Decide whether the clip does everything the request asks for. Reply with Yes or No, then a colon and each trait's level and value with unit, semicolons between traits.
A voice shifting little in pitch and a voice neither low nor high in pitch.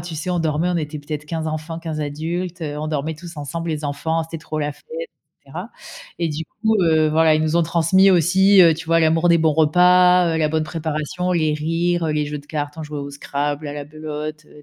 Yes: narrow, 1.9 semitones; medium, 160 Hz